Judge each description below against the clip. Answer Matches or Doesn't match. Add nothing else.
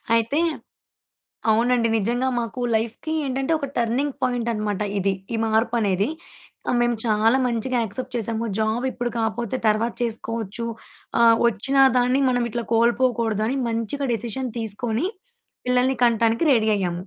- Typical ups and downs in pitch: Doesn't match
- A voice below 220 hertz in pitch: Doesn't match